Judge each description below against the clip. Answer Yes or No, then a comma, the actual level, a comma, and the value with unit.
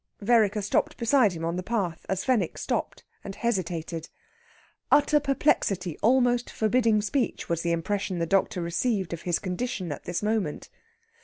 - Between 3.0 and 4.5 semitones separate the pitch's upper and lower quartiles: No, wide, 5.4 semitones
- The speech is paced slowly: No, average, 155 wpm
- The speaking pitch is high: Yes, high, 200 Hz